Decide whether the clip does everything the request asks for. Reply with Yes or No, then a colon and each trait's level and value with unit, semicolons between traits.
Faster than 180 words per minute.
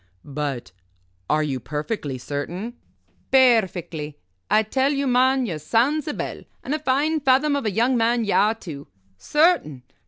No: average, 155 wpm